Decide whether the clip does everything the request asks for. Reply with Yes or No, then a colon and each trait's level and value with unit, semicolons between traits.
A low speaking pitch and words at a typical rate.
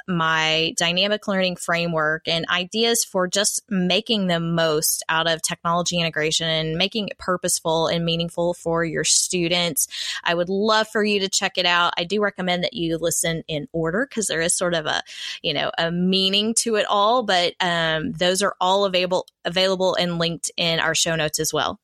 No: medium, 175 Hz; average, 190 wpm